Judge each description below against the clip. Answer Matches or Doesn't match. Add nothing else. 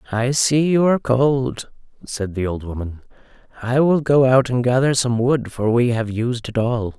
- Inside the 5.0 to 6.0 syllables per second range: Doesn't match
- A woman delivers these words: Doesn't match